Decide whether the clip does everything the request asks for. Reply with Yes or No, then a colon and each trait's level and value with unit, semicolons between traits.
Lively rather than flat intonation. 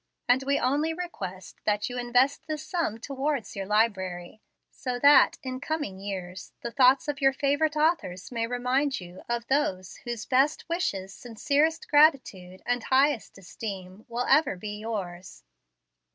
Yes: wide, 6.3 semitones